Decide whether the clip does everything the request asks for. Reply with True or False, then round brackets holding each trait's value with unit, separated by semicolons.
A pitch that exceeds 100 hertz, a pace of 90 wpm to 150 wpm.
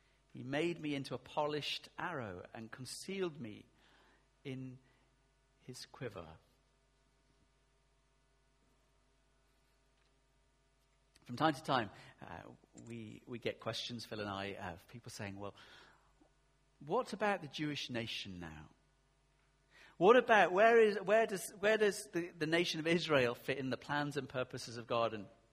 True (135 Hz; 135 wpm)